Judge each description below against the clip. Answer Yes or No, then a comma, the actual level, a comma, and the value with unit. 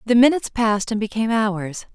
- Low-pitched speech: No, high, 220 Hz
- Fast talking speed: No, average, 185 wpm